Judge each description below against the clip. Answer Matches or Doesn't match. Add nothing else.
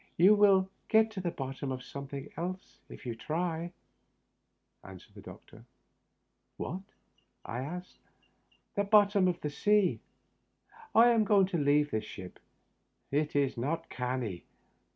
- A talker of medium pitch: Matches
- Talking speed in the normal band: Matches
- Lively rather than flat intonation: Matches